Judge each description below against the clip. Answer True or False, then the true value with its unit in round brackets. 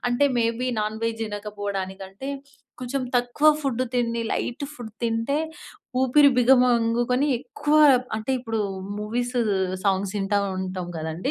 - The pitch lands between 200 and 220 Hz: False (230 Hz)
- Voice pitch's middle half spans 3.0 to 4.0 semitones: True (3.5 semitones)